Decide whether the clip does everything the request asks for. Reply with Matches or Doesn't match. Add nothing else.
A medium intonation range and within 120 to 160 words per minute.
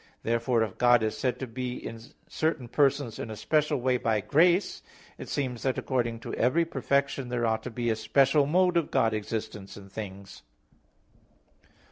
Doesn't match